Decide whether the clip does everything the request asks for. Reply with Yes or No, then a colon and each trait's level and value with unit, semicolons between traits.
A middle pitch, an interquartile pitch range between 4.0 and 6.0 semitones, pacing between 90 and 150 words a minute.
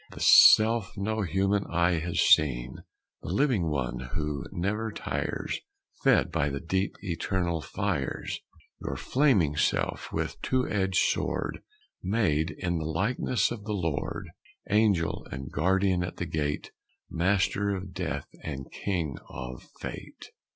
No: very low, 90 Hz; average, 4.6 semitones; slow, 135 wpm